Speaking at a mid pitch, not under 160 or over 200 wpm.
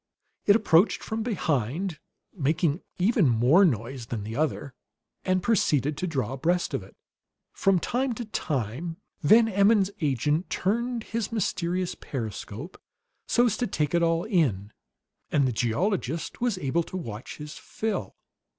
No: medium, 170 Hz; average, 145 wpm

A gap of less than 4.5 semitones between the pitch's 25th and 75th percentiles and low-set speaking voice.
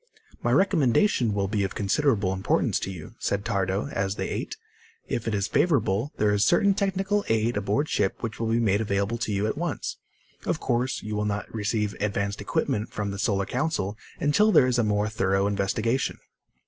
Yes: average, 3.7 semitones; low, 105 Hz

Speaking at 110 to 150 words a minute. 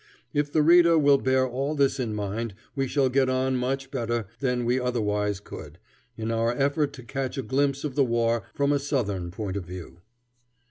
No: average, 195 wpm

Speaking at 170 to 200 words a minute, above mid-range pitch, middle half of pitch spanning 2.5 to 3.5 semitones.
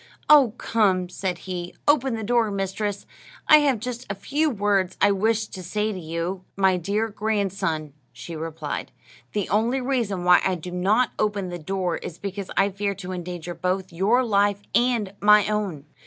Yes: average, 175 wpm; high, 200 Hz; average, 3.2 semitones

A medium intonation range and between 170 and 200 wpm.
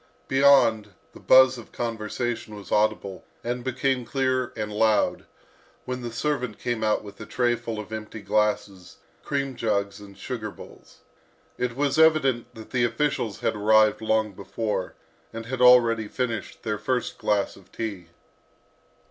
No: average, 3.0 semitones; average, 150 wpm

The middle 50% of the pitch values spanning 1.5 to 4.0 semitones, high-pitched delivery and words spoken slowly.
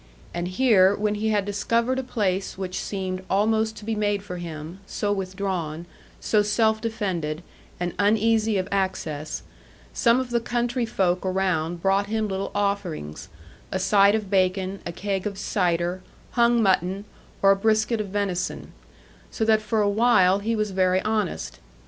No: average, 2.8 semitones; high, 200 Hz; average, 165 wpm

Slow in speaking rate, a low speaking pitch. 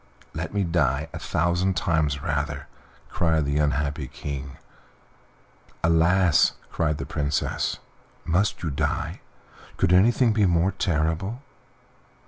Yes: slow, 110 wpm; very low, 80 Hz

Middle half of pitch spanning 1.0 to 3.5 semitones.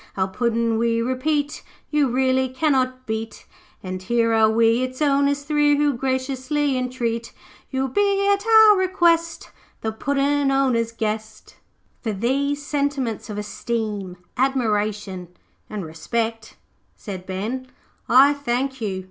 No: average, 4.2 semitones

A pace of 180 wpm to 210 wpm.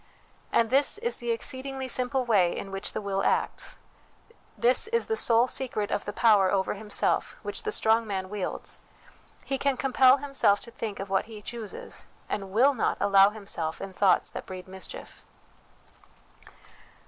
No: average, 165 wpm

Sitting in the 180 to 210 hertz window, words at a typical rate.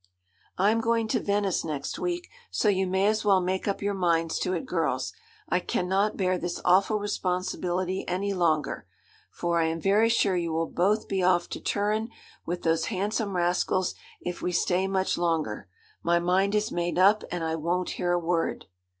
Yes: medium, 185 Hz; average, 185 wpm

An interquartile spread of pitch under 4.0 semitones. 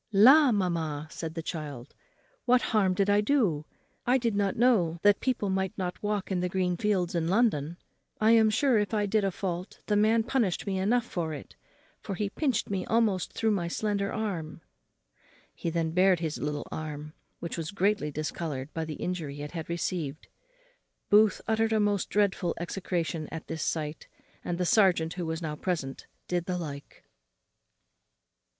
No: average, 4.4 semitones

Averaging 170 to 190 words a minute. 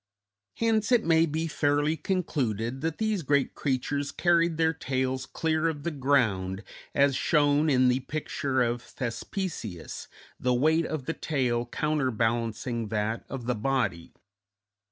No: slow, 135 wpm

